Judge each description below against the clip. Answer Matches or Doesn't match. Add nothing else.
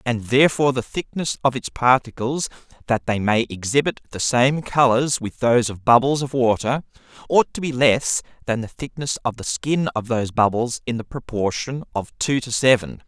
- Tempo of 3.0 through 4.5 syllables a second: Doesn't match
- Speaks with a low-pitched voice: Matches